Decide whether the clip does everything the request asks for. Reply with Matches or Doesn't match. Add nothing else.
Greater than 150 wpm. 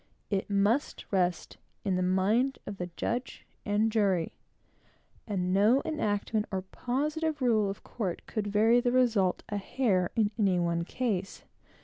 Doesn't match